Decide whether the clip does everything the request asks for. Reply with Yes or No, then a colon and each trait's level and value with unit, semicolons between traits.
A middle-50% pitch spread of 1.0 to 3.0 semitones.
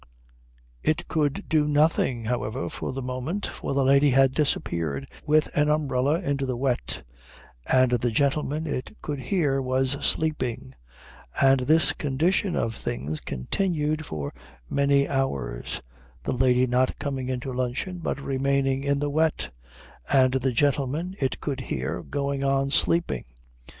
Yes: narrow, 2.6 semitones